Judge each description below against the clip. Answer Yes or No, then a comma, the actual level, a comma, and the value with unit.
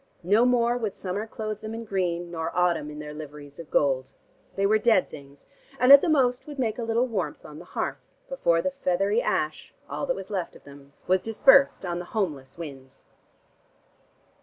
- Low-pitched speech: No, high, 190 Hz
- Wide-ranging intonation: Yes, wide, 6.9 semitones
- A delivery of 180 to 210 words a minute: Yes, average, 195 wpm